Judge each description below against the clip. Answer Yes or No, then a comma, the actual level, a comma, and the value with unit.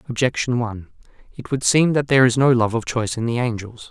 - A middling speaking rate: No, fast, 230 wpm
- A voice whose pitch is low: Yes, low, 120 Hz